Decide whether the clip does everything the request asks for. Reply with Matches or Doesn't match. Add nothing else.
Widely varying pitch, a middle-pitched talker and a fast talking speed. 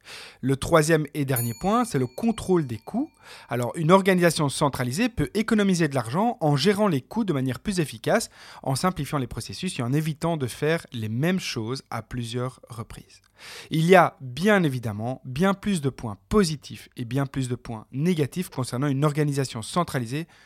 Doesn't match